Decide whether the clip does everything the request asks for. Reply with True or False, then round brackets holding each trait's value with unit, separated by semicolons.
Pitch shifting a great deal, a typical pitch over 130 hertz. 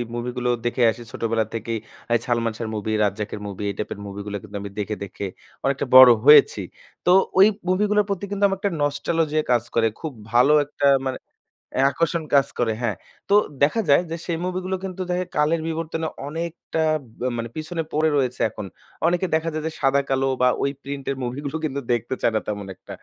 True (5.9 semitones; 140 Hz)